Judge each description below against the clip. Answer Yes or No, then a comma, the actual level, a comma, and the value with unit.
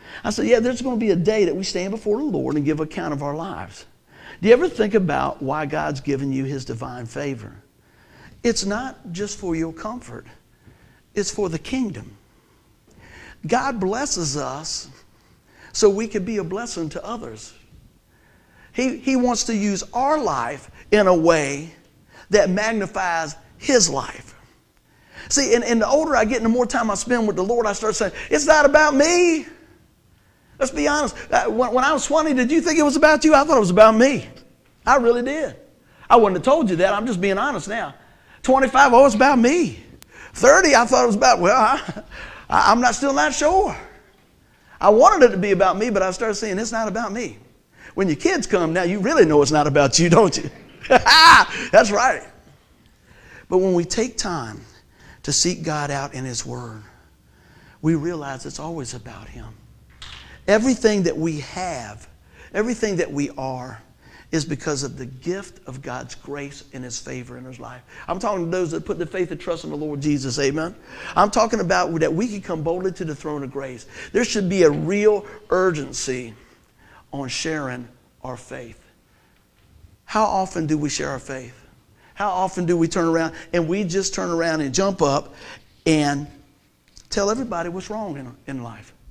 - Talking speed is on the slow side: No, average, 190 wpm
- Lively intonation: Yes, wide, 7.8 semitones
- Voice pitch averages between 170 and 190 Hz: Yes, medium, 185 Hz